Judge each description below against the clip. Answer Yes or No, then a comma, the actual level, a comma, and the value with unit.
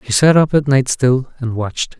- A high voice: No, low, 130 Hz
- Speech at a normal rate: No, fast, 240 wpm